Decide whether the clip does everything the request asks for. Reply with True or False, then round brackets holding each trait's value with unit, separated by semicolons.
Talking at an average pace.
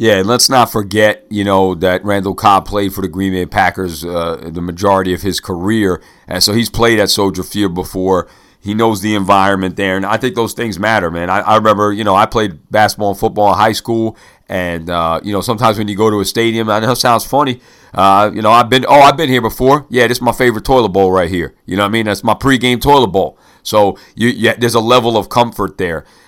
False (250 wpm)